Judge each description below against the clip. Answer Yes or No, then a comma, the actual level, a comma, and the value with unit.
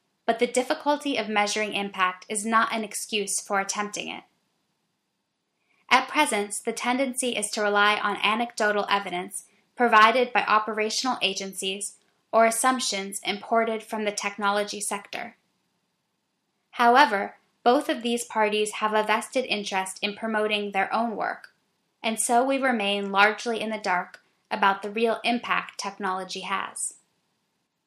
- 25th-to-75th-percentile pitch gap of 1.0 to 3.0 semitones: Yes, narrow, 2.5 semitones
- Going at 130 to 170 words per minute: Yes, slow, 135 wpm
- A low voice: No, high, 215 Hz